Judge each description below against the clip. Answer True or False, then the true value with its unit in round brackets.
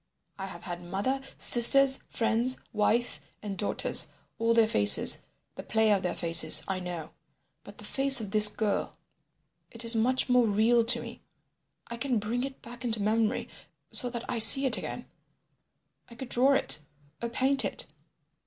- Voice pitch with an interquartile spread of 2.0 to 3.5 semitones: True (3.1 semitones)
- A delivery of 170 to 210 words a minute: False (160 wpm)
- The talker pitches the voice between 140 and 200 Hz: False (230 Hz)